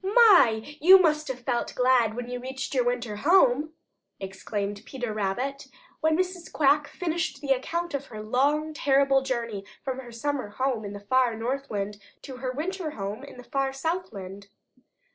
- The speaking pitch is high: Yes, very high, 260 Hz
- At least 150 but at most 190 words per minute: Yes, average, 165 wpm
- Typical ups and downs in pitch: Yes, average, 4.8 semitones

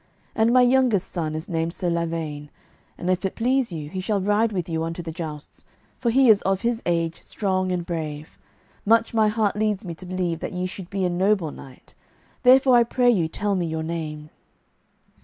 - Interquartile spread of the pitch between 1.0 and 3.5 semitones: No, average, 4.7 semitones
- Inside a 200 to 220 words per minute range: Yes, fast, 205 wpm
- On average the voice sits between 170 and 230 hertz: Yes, medium, 185 Hz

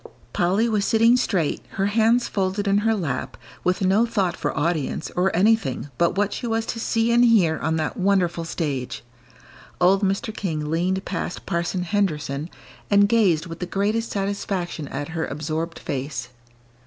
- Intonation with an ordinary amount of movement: Yes, average, 4.2 semitones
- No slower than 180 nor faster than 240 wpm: No, average, 165 wpm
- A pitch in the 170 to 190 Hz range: Yes, medium, 185 Hz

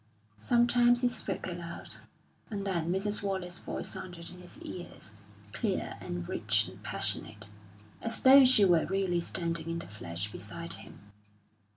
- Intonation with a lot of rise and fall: No, average, 4.1 semitones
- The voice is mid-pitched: Yes, medium, 180 Hz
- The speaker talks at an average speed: Yes, average, 150 wpm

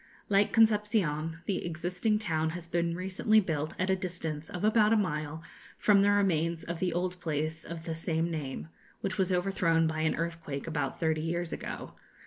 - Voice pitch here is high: No, medium, 170 Hz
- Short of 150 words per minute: No, average, 180 wpm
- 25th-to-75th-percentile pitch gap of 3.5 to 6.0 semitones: No, average, 3.0 semitones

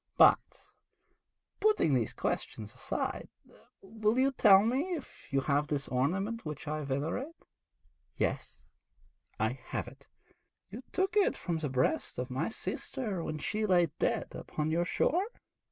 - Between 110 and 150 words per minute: Yes, average, 140 wpm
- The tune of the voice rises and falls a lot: Yes, wide, 9.0 semitones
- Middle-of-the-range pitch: Yes, medium, 175 Hz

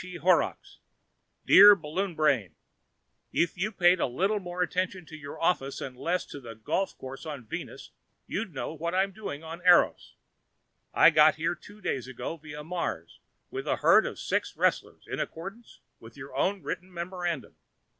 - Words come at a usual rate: Yes, average, 175 wpm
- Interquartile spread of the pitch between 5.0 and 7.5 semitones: No, average, 4.0 semitones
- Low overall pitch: No, medium, 170 Hz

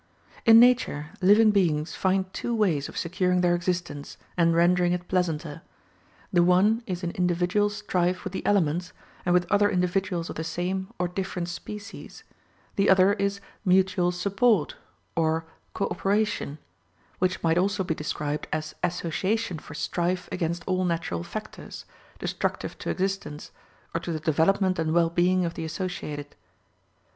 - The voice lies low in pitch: No, medium, 180 Hz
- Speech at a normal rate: Yes, average, 150 wpm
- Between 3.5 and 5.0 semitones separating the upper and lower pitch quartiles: No, narrow, 2.4 semitones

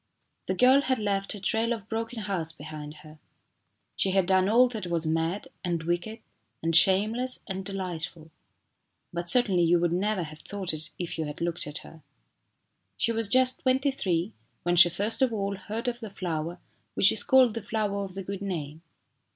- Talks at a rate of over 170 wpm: Yes, average, 190 wpm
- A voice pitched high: Yes, high, 195 Hz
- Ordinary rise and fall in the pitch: Yes, average, 4.7 semitones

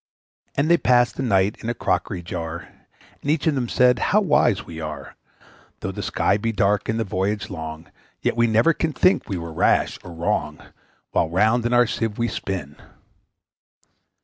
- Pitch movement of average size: No, wide, 5.9 semitones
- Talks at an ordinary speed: Yes, average, 190 wpm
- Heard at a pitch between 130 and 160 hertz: No, low, 105 Hz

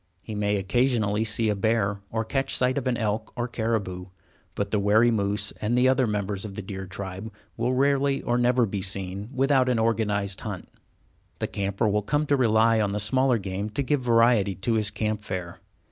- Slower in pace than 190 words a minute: No, average, 200 wpm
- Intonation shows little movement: No, average, 3.2 semitones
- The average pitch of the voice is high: No, low, 110 Hz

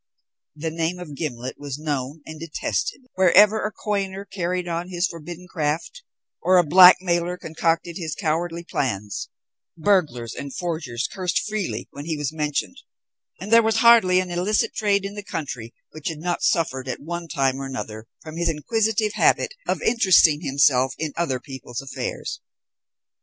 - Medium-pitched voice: Yes, medium, 165 Hz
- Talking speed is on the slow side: No, average, 160 wpm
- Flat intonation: No, average, 4.2 semitones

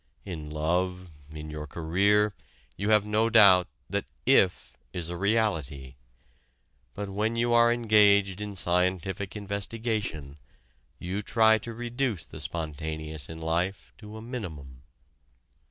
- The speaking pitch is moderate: No, very low, 95 Hz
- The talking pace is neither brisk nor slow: No, slow, 125 wpm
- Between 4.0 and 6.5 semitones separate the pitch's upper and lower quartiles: Yes, average, 4.9 semitones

